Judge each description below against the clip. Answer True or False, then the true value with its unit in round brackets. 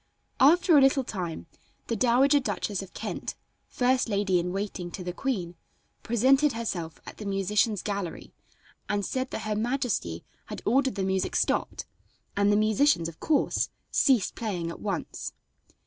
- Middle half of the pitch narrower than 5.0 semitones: False (5.4 semitones)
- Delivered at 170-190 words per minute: False (155 wpm)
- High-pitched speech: True (210 Hz)